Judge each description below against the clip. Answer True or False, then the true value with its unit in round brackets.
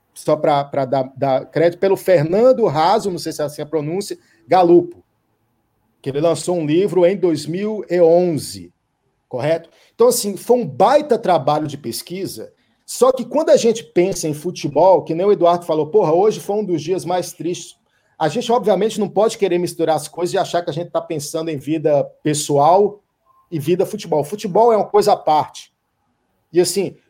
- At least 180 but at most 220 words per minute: True (185 wpm)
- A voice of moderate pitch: True (175 Hz)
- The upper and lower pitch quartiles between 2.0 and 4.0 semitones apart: False (4.7 semitones)